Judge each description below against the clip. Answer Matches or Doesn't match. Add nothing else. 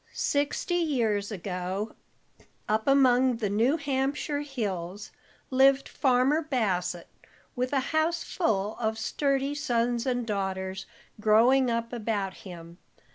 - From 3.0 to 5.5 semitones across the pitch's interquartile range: Matches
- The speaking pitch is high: Matches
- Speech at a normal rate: Doesn't match